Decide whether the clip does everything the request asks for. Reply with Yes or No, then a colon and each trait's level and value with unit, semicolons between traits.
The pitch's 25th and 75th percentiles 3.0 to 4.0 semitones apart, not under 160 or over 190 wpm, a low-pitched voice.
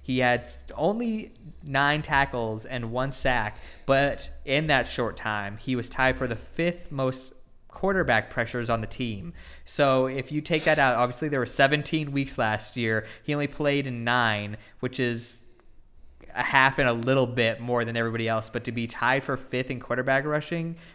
Yes: average, 3.3 semitones; average, 185 wpm; low, 125 Hz